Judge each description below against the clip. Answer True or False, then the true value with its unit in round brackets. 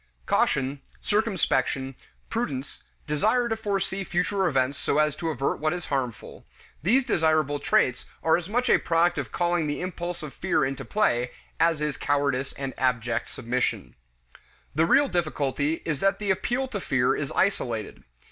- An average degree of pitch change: False (5.8 semitones)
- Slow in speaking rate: False (155 wpm)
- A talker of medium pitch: True (155 Hz)